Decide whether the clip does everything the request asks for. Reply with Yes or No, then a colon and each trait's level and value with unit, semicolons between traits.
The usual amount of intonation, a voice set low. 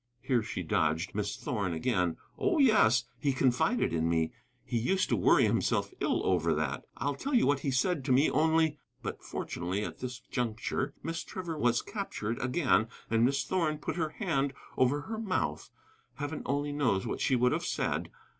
No: wide, 6.5 semitones; low, 130 Hz